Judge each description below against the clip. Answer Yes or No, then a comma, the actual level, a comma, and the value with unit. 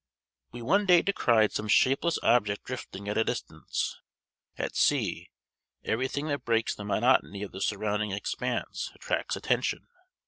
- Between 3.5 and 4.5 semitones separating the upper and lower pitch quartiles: Yes, average, 4.2 semitones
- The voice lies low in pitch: Yes, low, 110 Hz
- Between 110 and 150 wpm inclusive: Yes, average, 145 wpm